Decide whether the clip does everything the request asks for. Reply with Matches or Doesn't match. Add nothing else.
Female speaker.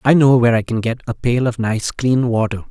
Doesn't match